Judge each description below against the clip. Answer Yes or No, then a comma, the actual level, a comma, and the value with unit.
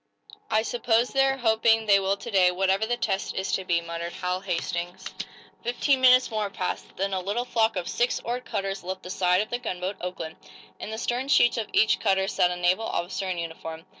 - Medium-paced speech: No, fast, 210 wpm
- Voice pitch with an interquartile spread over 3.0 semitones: Yes, average, 4.1 semitones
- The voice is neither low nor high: No, high, 195 Hz